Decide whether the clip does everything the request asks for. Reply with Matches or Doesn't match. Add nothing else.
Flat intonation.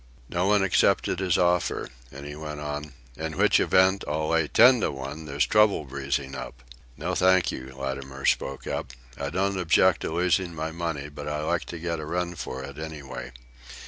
Doesn't match